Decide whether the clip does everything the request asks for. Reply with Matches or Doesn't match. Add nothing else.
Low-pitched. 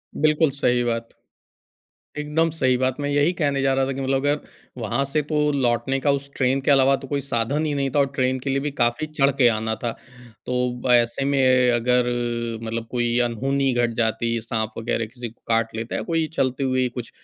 Matches